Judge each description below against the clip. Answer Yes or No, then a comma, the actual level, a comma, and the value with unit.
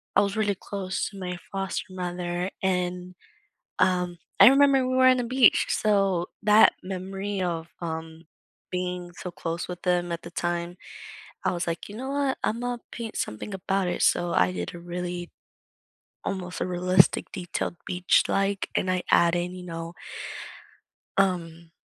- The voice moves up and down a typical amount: No, narrow, 2.1 semitones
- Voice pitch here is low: No, medium, 180 Hz